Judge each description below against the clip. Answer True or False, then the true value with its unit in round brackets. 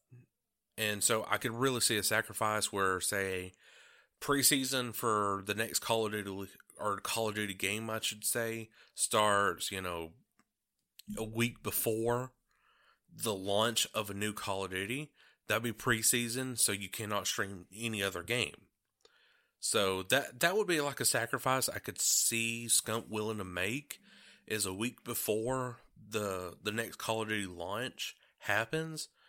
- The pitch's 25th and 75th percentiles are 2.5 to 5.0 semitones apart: True (2.9 semitones)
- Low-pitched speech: True (110 Hz)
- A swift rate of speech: False (155 wpm)